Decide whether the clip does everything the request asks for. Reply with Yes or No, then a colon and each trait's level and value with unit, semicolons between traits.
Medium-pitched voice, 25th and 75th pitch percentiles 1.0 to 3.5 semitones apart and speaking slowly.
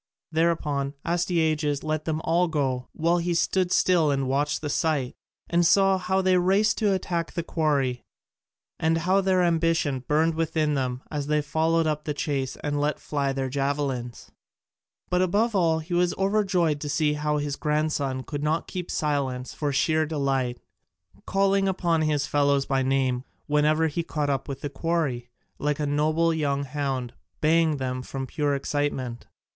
No: medium, 150 Hz; average, 3.0 semitones; average, 165 wpm